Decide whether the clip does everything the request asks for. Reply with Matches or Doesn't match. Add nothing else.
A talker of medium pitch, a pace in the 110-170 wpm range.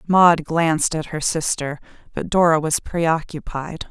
Matches